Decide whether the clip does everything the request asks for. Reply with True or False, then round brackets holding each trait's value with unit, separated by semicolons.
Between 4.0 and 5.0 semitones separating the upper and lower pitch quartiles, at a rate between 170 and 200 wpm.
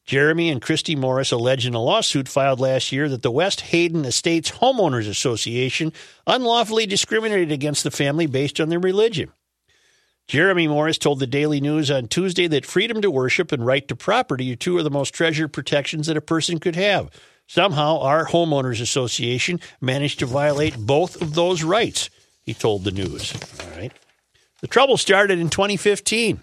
True (4.4 semitones; 175 wpm)